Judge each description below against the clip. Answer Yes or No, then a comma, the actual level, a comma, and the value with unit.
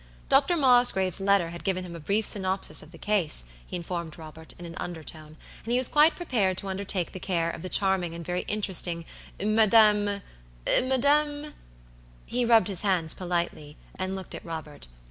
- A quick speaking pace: No, average, 170 wpm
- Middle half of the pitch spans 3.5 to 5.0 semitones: Yes, average, 4.1 semitones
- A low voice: No, high, 190 Hz